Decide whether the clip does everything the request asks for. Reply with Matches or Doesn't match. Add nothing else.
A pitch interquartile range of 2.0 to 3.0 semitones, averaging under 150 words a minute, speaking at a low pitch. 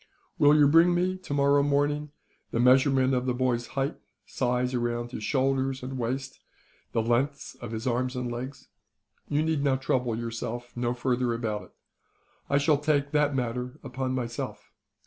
Doesn't match